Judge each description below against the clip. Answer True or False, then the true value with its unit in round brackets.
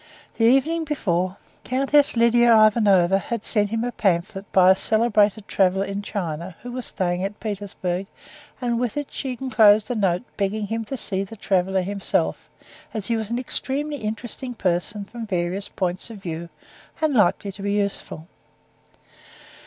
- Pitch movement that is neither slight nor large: True (3.8 semitones)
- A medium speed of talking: True (160 wpm)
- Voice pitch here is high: True (205 Hz)